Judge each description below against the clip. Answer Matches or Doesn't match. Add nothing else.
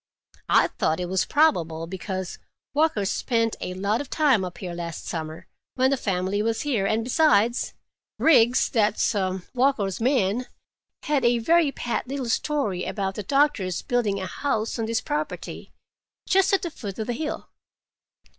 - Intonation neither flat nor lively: Doesn't match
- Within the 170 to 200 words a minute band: Doesn't match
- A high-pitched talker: Matches